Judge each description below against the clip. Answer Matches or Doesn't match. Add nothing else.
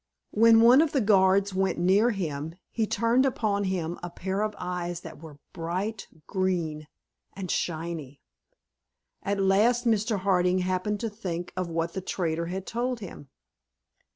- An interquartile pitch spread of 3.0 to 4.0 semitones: Matches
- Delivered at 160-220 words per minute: Doesn't match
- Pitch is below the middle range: Doesn't match